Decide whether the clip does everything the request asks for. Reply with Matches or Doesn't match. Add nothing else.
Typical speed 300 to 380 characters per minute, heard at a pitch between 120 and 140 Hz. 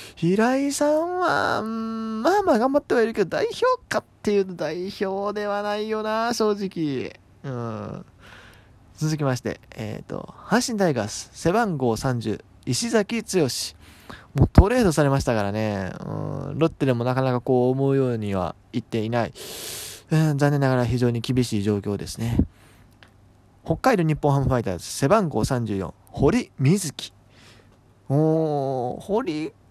Doesn't match